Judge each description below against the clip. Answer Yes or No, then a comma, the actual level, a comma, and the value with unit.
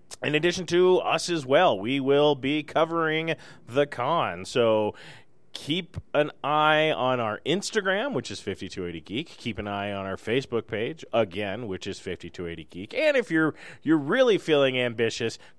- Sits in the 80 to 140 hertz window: Yes, low, 135 Hz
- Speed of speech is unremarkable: Yes, average, 160 wpm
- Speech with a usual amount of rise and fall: No, wide, 7.2 semitones